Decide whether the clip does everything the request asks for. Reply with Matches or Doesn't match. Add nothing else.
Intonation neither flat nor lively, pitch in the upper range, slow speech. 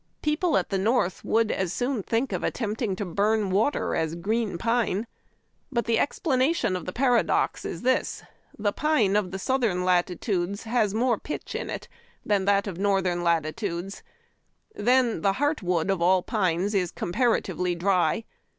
Doesn't match